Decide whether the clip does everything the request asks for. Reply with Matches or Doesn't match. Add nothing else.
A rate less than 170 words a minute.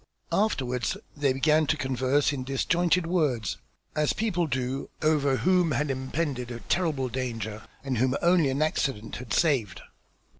Matches